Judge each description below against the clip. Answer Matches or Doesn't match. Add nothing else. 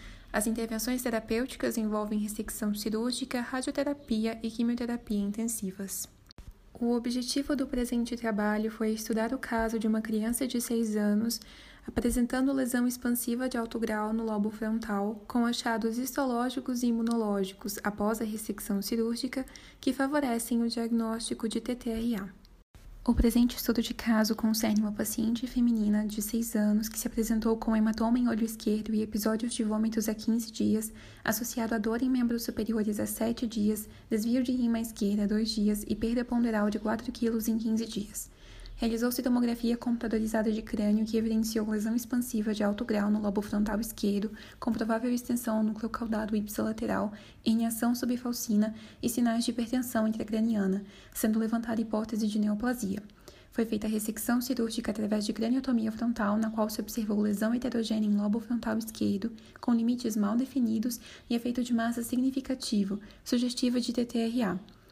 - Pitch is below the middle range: Doesn't match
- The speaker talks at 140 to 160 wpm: Matches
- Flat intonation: Matches